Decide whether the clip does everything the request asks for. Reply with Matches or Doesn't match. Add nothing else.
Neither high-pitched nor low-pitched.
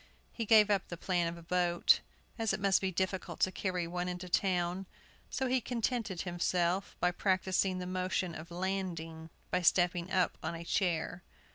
Matches